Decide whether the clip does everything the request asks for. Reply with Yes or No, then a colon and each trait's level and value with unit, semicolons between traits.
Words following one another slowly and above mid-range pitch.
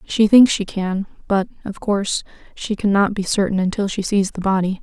No: average, 200 wpm; high, 200 Hz